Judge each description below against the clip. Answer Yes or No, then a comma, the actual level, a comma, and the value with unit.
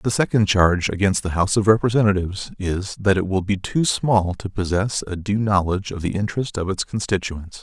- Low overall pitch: Yes, low, 100 Hz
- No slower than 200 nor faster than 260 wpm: Yes, fast, 205 wpm